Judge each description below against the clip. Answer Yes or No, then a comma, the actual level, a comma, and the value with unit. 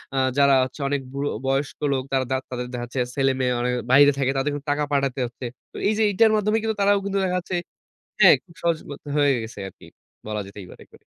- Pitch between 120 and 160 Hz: Yes, medium, 140 Hz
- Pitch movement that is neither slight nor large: Yes, average, 4.7 semitones